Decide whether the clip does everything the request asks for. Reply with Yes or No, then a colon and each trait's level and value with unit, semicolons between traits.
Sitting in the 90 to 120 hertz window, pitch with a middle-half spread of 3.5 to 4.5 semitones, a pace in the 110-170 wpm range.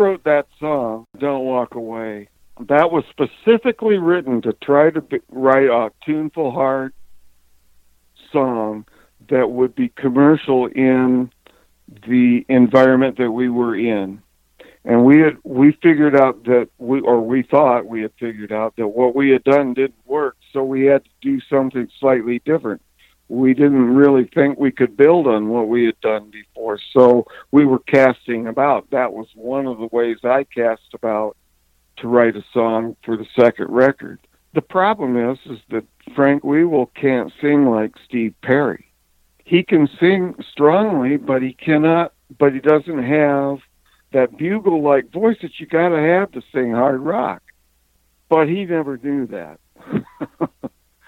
No: low, 130 Hz; average, 3.9 semitones; average, 160 wpm